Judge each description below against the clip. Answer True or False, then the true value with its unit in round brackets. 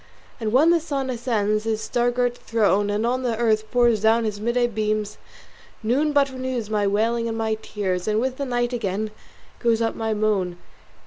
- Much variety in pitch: False (2.4 semitones)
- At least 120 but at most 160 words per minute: False (190 wpm)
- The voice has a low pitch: False (225 Hz)